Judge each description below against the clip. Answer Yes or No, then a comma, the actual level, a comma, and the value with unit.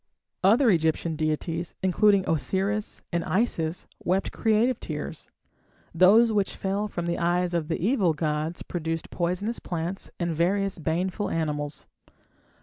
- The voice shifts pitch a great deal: No, average, 3.5 semitones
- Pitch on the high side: No, medium, 175 Hz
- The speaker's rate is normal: No, slow, 130 wpm